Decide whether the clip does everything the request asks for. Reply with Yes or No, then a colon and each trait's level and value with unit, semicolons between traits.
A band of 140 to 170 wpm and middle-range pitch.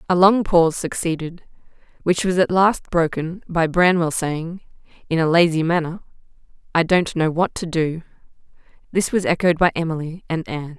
Yes: average, 160 wpm; medium, 170 Hz